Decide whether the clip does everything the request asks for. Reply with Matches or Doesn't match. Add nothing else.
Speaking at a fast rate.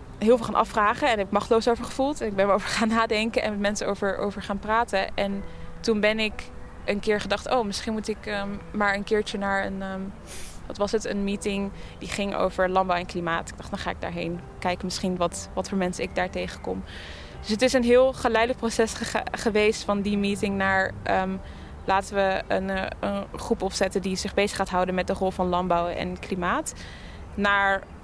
Matches